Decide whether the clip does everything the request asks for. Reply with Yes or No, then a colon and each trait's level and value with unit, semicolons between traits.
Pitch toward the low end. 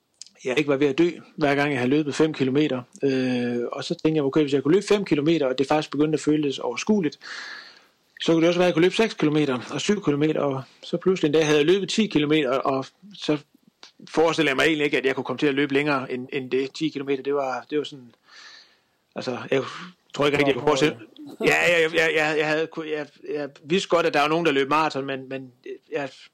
No: medium, 150 Hz